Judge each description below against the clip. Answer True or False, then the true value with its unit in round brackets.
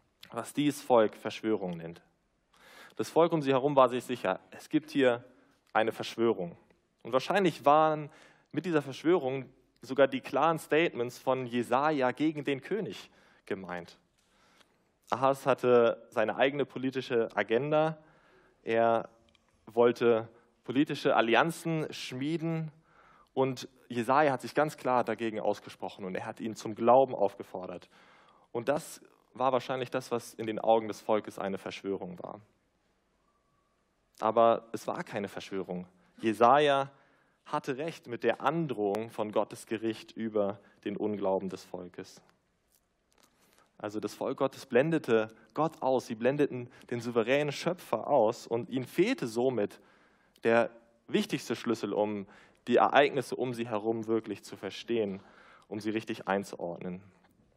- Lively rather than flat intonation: False (4.0 semitones)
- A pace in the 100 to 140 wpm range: True (130 wpm)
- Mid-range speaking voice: False (120 Hz)